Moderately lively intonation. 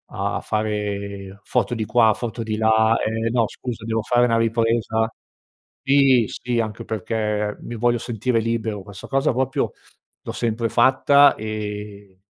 No: narrow, 2.0 semitones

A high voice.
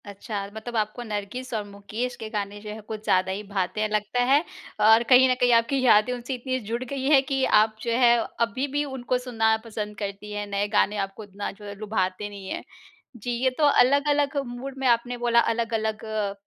Yes: high, 225 Hz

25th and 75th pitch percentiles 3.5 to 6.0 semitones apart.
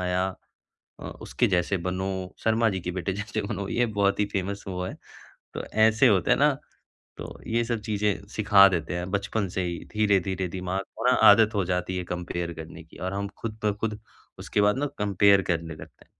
No: narrow, 2.6 semitones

